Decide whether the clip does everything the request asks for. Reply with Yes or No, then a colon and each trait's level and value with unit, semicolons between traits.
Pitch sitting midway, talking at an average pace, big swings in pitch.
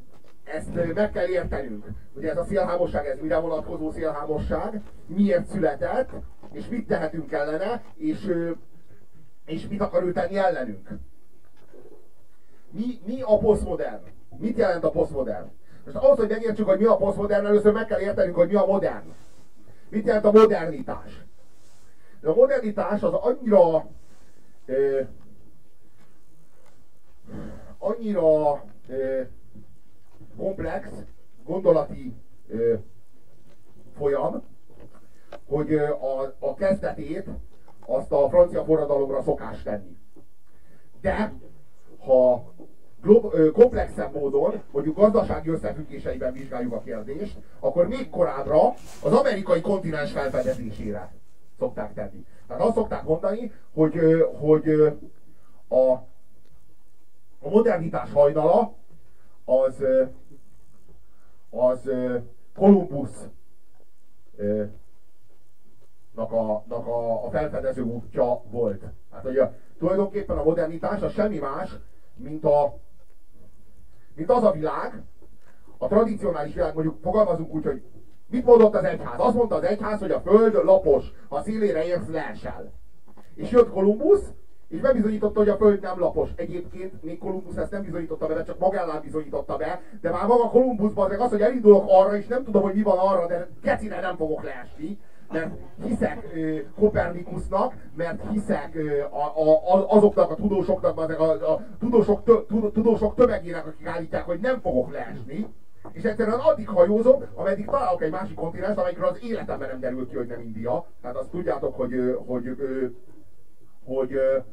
Yes: medium, 175 Hz; average, 130 wpm; wide, 7.5 semitones